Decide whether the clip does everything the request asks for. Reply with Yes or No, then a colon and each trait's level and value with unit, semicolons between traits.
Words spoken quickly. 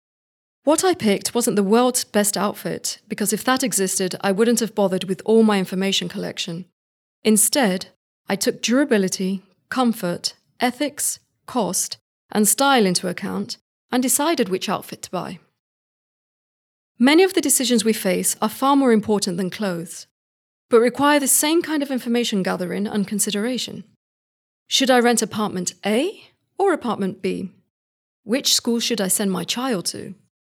No: average, 150 wpm